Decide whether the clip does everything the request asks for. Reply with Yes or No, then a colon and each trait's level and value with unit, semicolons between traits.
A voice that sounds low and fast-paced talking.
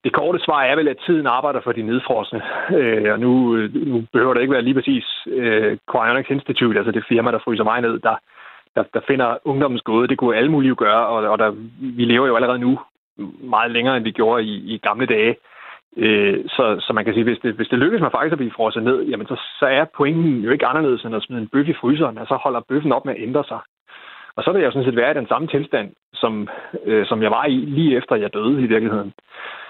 Yes: low, 120 Hz; fast, 250 wpm